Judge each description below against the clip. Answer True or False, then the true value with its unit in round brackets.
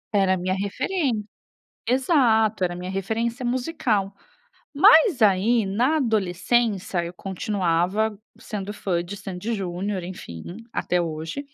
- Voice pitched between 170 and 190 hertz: False (200 Hz)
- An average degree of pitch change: True (4.2 semitones)